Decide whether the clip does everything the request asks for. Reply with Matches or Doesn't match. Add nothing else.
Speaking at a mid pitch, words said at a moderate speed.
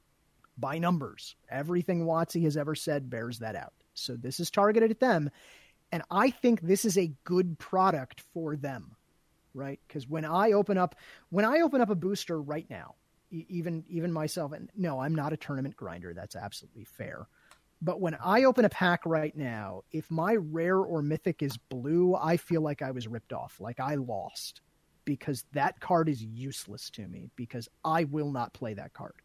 Matches